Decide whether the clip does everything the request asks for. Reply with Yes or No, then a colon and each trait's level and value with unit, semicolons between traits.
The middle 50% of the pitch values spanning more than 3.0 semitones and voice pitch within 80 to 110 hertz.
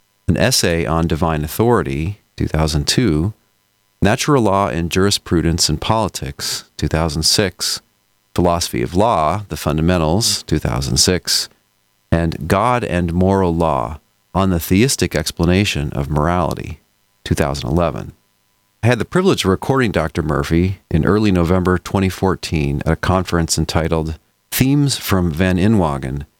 Yes: average, 3.8 semitones; very low, 90 Hz